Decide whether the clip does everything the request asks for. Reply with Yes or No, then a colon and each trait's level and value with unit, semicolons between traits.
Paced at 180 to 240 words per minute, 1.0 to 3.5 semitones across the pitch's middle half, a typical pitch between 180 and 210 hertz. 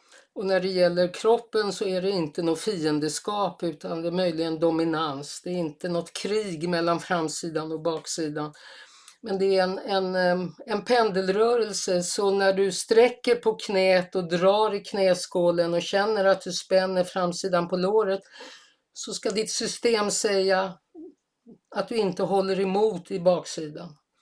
No: average, 155 wpm; average, 3.1 semitones; high, 190 Hz